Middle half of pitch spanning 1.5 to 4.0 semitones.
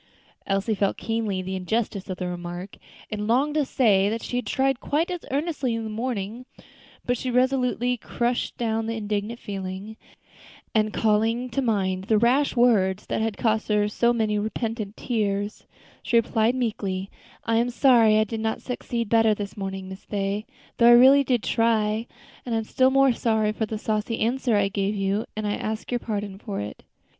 Yes: average, 2.8 semitones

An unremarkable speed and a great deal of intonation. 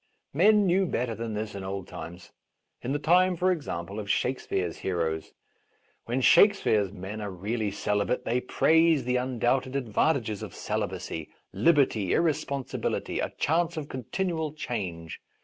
Yes: average, 150 wpm; wide, 7.8 semitones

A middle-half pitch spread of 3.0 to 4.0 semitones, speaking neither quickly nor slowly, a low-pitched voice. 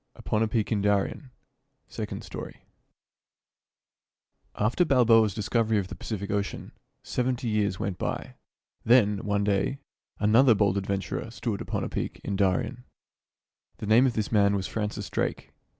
No: narrow, 2.4 semitones; average, 150 wpm; low, 105 Hz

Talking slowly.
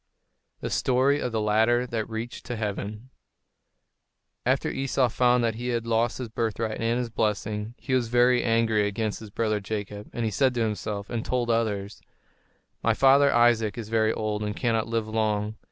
No: average, 180 wpm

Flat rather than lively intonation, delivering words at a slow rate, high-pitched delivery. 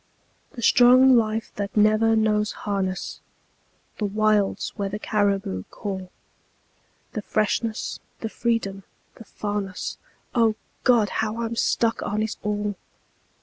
Yes: narrow, 1.9 semitones; slow, 120 wpm; high, 215 Hz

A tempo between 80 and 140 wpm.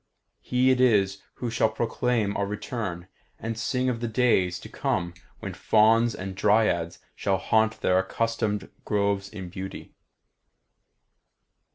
Yes: slow, 135 wpm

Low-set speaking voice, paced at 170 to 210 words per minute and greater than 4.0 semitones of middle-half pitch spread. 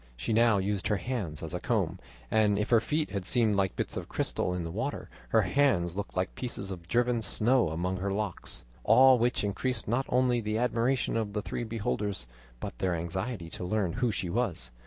Yes: low, 105 Hz; fast, 205 wpm; average, 4.5 semitones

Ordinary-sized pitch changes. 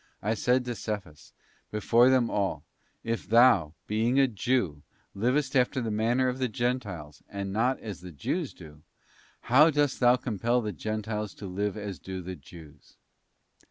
Yes: average, 4.4 semitones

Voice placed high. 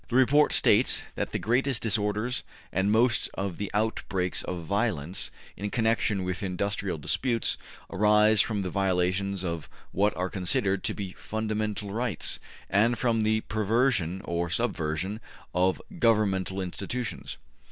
No: low, 100 Hz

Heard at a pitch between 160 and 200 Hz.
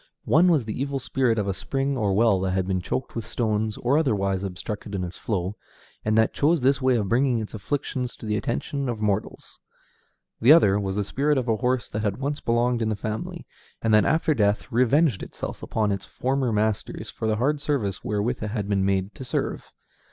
No: low, 110 Hz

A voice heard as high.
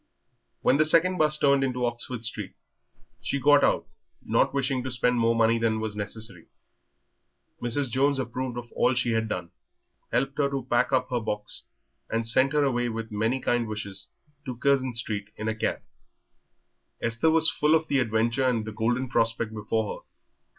No: low, 120 Hz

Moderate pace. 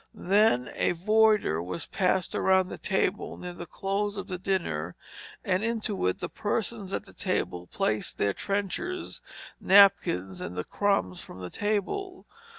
Yes: average, 155 wpm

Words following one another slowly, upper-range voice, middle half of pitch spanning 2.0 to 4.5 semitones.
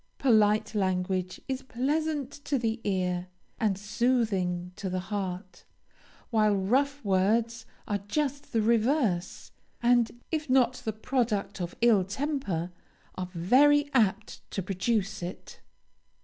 No: slow, 120 wpm; high, 215 Hz; average, 5.2 semitones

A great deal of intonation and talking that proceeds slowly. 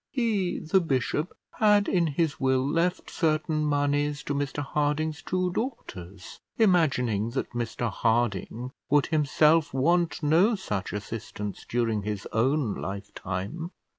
Yes: wide, 6.2 semitones; slow, 125 wpm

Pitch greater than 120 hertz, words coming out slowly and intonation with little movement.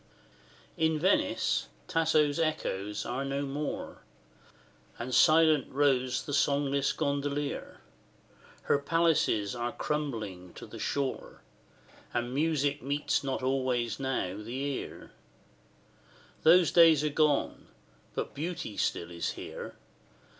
No: medium, 140 Hz; slow, 110 wpm; average, 3.2 semitones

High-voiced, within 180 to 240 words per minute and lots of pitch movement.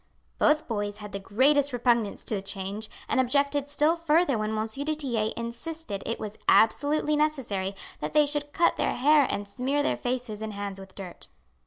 Yes: high, 245 Hz; average, 185 wpm; wide, 5.9 semitones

